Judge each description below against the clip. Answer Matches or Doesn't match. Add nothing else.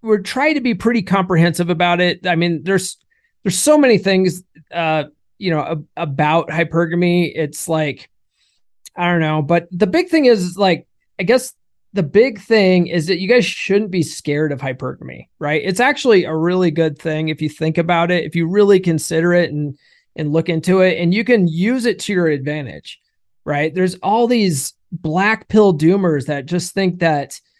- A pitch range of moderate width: Matches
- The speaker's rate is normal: Matches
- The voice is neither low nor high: Matches